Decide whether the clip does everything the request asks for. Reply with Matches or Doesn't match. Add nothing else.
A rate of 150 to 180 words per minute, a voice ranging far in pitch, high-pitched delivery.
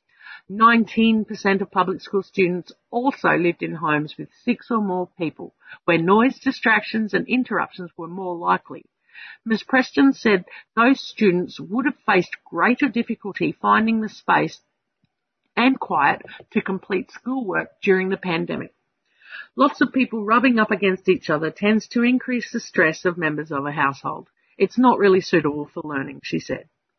Doesn't match